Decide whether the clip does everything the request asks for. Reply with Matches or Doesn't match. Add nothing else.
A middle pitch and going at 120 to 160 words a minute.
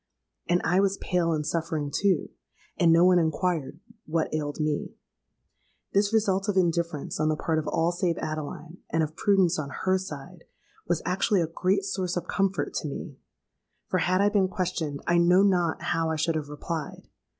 Doesn't match